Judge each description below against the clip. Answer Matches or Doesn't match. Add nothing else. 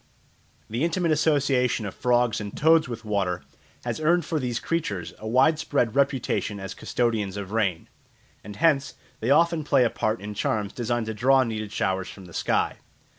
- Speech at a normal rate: Matches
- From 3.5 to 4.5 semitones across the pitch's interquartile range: Doesn't match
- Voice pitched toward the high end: Doesn't match